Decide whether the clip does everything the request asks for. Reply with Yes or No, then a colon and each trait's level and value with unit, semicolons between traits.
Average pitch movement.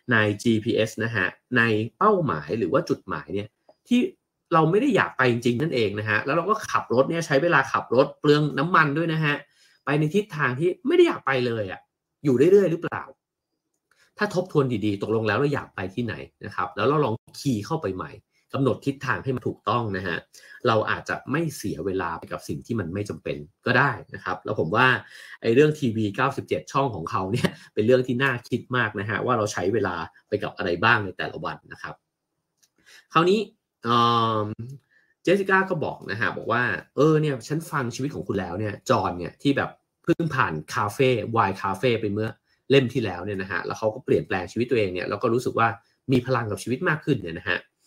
No: wide, 6.0 semitones